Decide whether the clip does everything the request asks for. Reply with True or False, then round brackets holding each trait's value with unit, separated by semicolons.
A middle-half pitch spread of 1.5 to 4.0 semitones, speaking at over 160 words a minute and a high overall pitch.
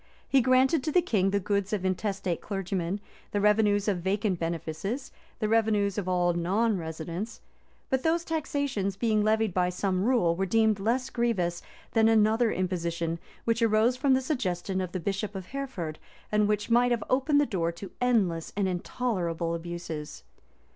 False (4.5 semitones; 170 wpm; 205 Hz)